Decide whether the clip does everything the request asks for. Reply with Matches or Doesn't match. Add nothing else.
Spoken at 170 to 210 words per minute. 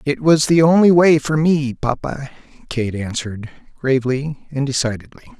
Doesn't match